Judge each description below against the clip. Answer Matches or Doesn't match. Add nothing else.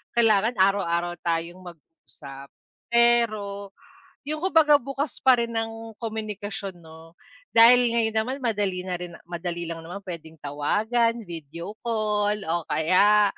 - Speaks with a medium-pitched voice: Doesn't match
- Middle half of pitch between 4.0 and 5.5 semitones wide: Matches